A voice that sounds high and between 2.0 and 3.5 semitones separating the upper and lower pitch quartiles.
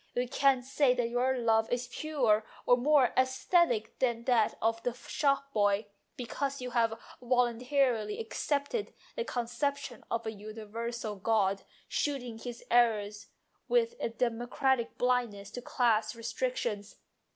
Yes: high, 240 Hz; average, 2.9 semitones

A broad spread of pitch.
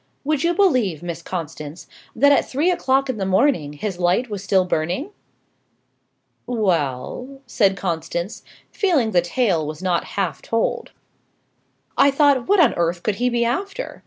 Yes: wide, 7.8 semitones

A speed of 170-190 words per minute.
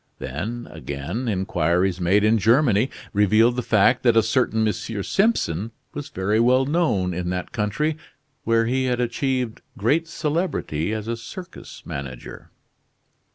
No: average, 140 wpm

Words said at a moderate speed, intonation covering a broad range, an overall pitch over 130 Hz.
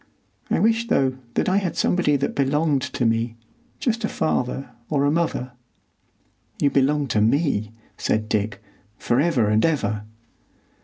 Yes: average, 145 wpm; wide, 6.2 semitones; medium, 140 Hz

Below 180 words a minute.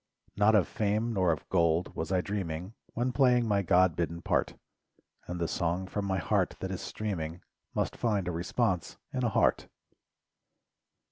Yes: average, 165 wpm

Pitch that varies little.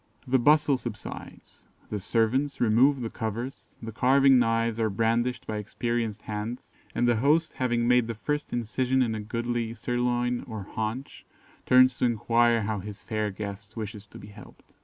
Yes: narrow, 2.3 semitones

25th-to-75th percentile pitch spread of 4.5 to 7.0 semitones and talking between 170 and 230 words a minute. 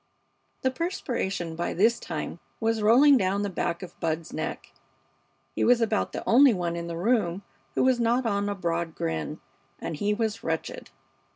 Yes: wide, 5.5 semitones; average, 175 wpm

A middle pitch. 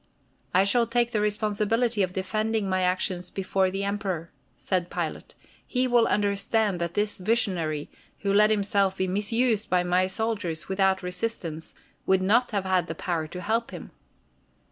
No: high, 195 Hz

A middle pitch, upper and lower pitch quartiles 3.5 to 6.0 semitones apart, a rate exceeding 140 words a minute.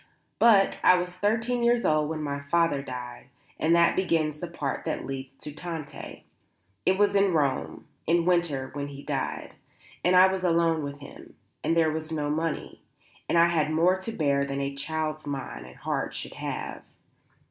Yes: medium, 160 Hz; average, 3.9 semitones; average, 180 wpm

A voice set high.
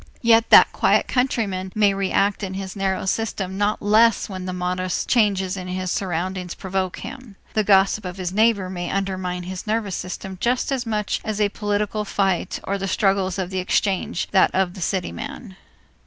Yes: high, 195 Hz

